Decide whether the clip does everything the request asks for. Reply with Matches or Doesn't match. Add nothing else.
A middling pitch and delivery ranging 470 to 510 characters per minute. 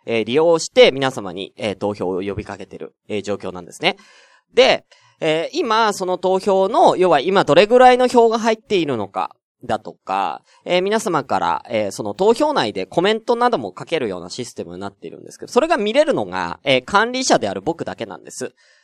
Doesn't match